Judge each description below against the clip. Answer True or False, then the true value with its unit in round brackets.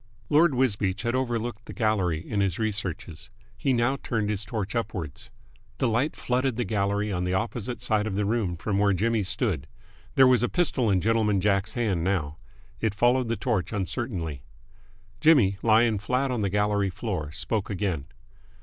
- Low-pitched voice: True (105 Hz)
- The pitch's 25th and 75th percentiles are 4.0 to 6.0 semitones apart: False (3.6 semitones)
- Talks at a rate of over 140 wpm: True (175 wpm)